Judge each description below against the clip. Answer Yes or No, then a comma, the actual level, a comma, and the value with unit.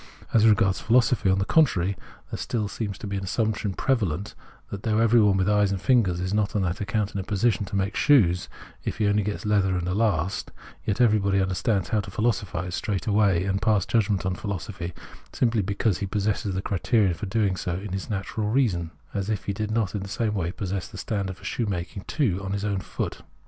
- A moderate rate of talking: No, fast, 215 wpm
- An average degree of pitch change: No, narrow, 2.3 semitones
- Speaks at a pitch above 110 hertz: No, low, 100 Hz